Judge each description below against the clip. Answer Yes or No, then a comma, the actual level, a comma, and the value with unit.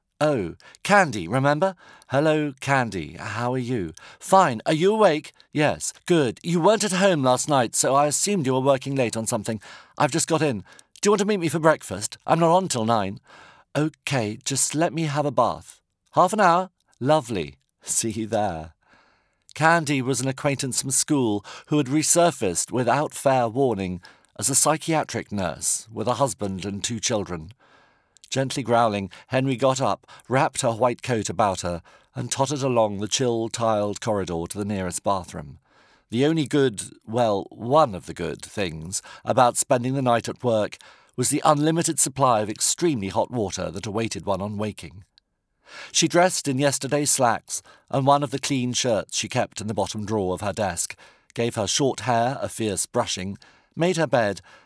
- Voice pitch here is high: No, low, 130 Hz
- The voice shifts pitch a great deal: Yes, wide, 5.8 semitones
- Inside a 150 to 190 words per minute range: Yes, average, 180 wpm